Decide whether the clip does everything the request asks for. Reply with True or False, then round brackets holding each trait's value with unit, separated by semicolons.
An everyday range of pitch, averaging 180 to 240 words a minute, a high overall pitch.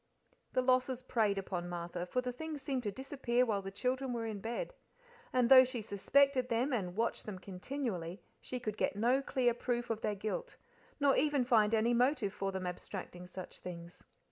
True (4.7 semitones; 190 wpm; 235 Hz)